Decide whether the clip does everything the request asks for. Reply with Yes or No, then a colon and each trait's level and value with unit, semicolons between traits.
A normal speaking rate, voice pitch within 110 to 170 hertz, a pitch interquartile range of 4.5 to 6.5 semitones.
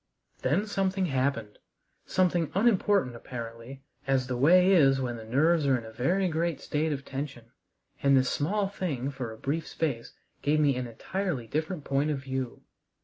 Yes: average, 170 wpm; medium, 140 Hz; average, 5.2 semitones